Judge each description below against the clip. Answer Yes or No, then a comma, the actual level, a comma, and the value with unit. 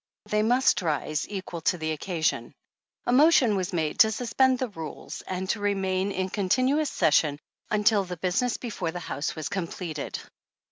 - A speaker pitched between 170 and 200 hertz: Yes, high, 190 Hz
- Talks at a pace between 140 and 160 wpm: No, average, 175 wpm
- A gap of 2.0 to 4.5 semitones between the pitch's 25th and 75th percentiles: No, average, 4.9 semitones